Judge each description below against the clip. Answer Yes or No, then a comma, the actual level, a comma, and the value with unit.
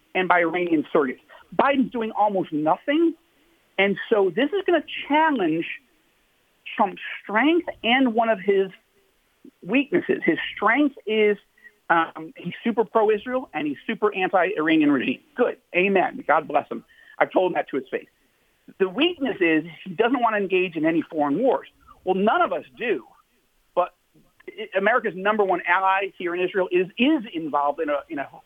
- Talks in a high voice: Yes, high, 220 Hz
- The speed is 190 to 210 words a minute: No, average, 165 wpm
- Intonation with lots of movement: Yes, wide, 7.9 semitones